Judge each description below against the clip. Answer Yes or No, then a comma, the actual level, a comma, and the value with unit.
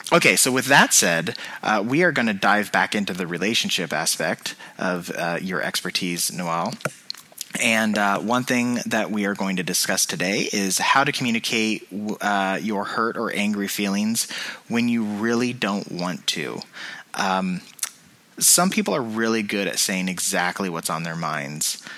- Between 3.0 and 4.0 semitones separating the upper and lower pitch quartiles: Yes, average, 3.5 semitones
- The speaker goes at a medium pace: Yes, average, 165 wpm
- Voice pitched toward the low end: Yes, low, 105 Hz